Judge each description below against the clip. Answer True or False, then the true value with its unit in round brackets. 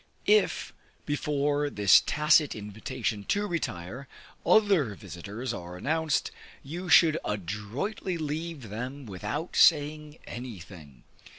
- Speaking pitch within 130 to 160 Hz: True (140 Hz)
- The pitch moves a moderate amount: False (7.1 semitones)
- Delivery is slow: True (100 wpm)